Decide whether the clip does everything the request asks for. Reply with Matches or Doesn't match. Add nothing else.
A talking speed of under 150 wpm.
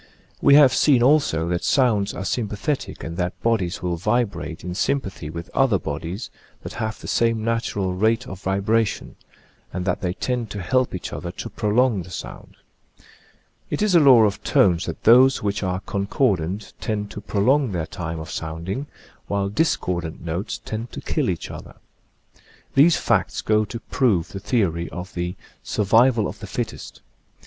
Doesn't match